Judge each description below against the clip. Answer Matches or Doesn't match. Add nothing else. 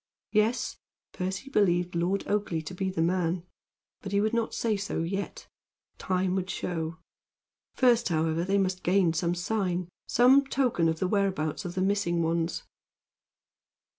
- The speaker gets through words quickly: Doesn't match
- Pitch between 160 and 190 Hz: Matches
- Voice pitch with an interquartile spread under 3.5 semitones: Matches